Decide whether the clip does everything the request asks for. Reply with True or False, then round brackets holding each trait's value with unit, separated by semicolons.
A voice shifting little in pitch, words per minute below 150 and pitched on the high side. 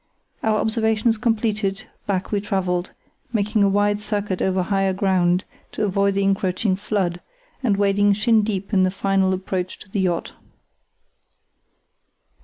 True (2.0 semitones; 140 wpm; 200 Hz)